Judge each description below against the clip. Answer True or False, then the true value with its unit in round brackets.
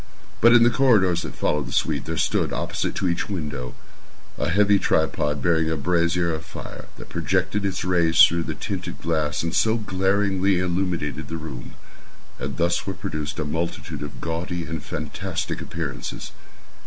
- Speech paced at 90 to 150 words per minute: False (165 wpm)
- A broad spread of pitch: False (3.3 semitones)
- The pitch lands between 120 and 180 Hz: False (85 Hz)